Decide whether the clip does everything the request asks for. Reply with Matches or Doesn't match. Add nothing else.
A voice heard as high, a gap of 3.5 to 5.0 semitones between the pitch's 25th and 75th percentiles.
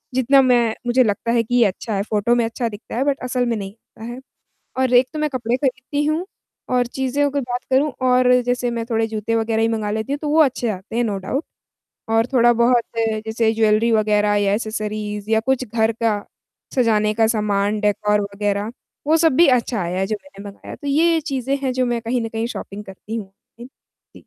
Doesn't match